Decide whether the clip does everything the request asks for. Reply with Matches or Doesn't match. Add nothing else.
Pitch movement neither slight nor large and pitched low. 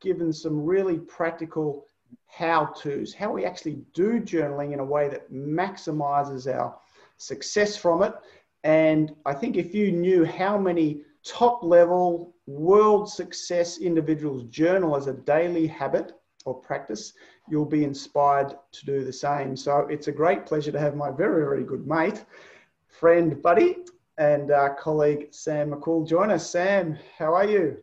Doesn't match